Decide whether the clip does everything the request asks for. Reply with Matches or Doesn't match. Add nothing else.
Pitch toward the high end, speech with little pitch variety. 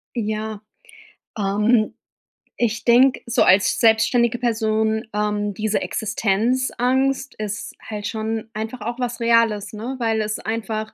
Matches